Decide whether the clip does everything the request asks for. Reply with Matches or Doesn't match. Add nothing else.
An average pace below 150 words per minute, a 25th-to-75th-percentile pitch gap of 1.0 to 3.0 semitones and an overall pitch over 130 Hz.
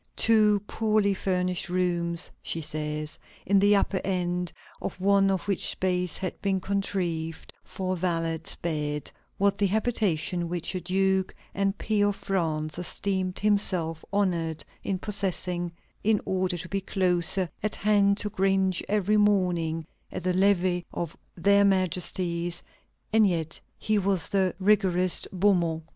Matches